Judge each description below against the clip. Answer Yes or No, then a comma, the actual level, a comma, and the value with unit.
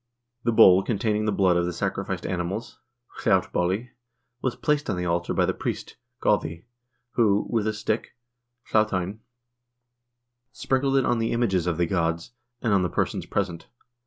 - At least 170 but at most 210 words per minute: No, average, 160 wpm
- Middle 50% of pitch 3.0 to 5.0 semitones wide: Yes, average, 4.5 semitones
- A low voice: Yes, low, 100 Hz